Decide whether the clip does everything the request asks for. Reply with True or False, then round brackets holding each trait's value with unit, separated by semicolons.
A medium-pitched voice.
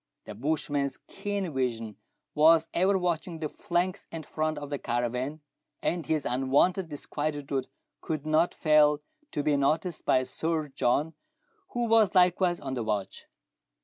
True (155 Hz)